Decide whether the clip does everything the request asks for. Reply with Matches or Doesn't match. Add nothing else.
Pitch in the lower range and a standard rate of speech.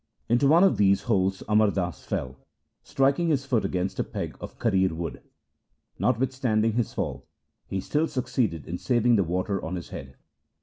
Matches